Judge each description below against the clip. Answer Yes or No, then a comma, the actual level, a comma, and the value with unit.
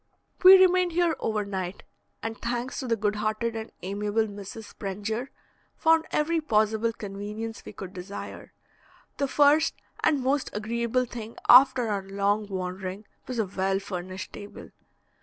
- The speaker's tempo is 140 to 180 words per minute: Yes, average, 145 wpm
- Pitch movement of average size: Yes, average, 4.0 semitones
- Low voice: No, high, 220 Hz